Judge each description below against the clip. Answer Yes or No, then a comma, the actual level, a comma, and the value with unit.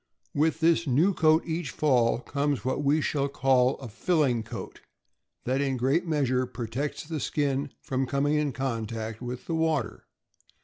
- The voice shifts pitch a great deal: No, average, 3.3 semitones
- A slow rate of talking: No, average, 165 wpm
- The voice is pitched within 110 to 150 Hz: Yes, medium, 140 Hz